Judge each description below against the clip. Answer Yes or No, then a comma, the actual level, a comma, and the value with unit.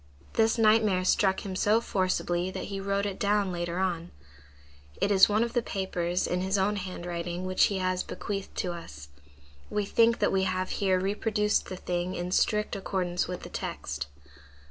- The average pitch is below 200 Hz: Yes, high, 190 Hz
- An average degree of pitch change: No, narrow, 2.3 semitones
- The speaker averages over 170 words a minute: Yes, average, 180 wpm